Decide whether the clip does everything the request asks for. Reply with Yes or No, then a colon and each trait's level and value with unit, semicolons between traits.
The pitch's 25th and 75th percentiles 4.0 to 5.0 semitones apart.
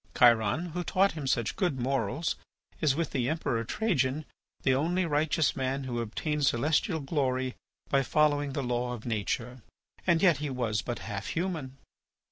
Yes: average, 4.3 semitones